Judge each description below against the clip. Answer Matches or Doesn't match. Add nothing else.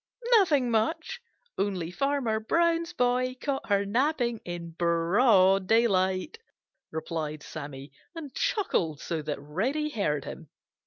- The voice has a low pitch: Doesn't match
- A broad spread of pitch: Matches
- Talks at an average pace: Doesn't match